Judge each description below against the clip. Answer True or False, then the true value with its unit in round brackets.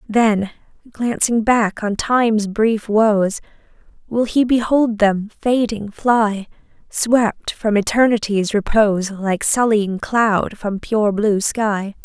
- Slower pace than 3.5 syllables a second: True (3.3 syllables/s)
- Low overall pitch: False (215 Hz)